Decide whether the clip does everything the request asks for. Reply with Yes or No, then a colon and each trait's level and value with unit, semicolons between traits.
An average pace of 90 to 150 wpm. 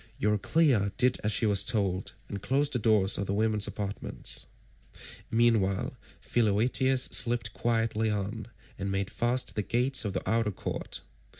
Yes: average, 145 wpm